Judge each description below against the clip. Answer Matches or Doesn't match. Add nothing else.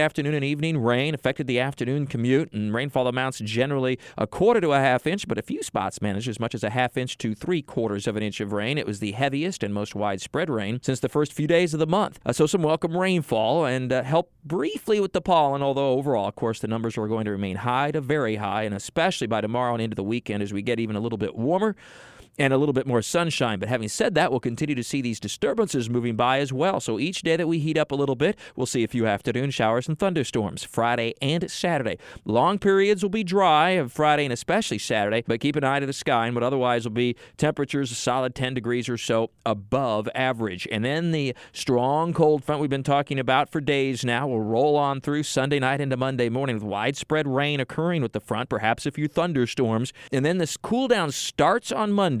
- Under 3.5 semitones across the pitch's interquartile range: Doesn't match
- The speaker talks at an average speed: Doesn't match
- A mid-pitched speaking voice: Doesn't match